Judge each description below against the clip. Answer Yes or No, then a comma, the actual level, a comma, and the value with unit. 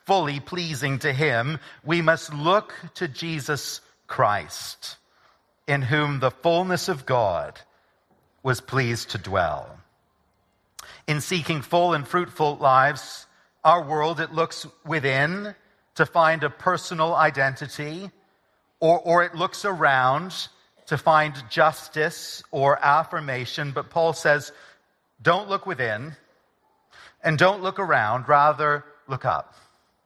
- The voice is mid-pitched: Yes, medium, 155 Hz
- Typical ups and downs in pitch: Yes, average, 3.4 semitones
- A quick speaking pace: No, slow, 120 wpm